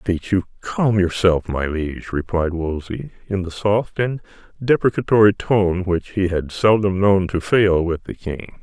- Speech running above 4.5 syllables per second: No, 4.4 syllables/s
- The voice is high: No, very low, 95 Hz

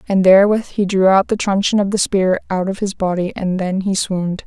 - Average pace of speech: No, fast, 240 wpm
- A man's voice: No, female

